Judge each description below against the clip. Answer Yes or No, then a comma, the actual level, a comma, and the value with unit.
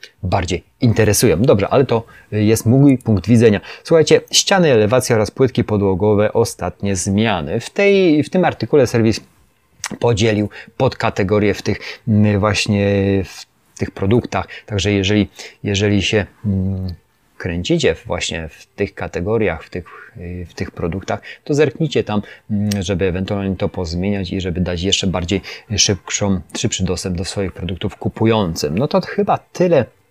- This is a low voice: Yes, low, 105 Hz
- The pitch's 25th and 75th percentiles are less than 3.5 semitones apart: Yes, average, 2.8 semitones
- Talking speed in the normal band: Yes, average, 135 wpm